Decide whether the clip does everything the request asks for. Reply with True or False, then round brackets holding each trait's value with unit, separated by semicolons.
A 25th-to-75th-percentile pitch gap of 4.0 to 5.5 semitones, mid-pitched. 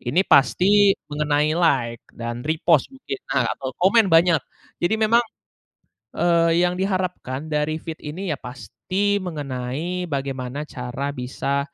True (5.0 semitones; 155 Hz)